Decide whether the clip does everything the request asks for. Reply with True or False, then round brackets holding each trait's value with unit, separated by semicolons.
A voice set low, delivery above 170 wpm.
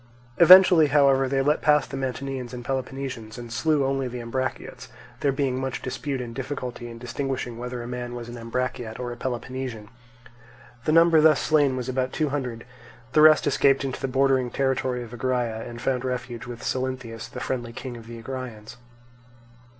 True (130 Hz; 180 wpm)